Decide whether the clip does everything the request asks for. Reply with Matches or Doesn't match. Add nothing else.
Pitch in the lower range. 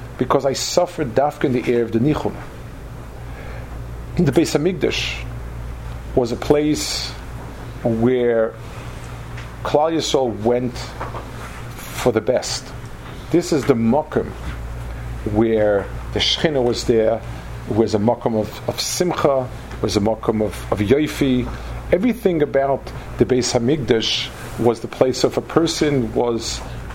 Matches